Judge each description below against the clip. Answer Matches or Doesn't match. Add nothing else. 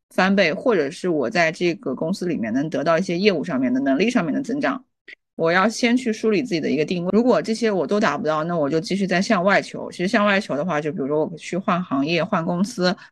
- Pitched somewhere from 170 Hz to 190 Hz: Matches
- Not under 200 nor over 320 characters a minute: Doesn't match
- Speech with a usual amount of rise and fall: Matches